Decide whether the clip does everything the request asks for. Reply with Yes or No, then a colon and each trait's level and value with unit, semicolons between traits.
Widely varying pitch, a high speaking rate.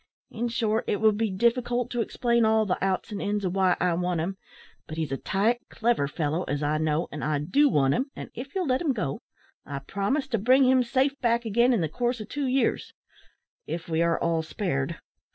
Yes: wide, 6.4 semitones; fast, 225 wpm